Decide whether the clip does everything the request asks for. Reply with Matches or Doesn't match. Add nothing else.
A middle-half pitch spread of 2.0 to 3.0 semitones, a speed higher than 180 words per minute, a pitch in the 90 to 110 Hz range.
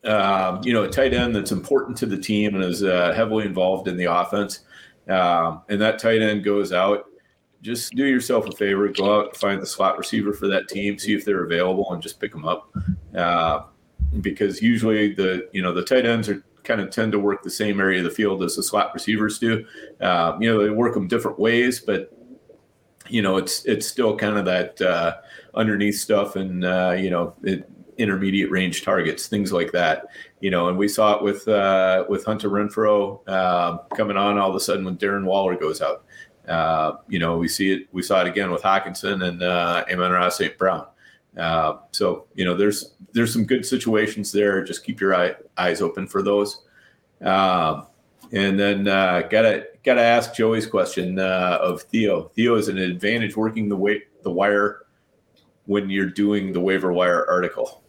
Matches